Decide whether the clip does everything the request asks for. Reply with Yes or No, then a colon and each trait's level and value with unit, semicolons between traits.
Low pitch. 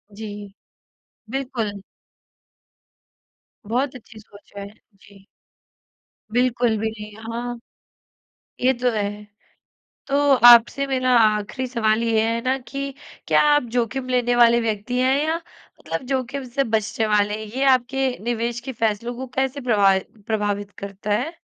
No: high, 235 Hz